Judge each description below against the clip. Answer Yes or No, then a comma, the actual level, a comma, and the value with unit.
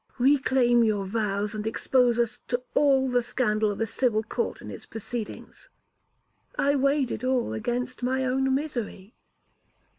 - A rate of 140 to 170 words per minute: Yes, average, 150 wpm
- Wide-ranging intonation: No, average, 3.2 semitones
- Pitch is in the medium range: No, high, 245 Hz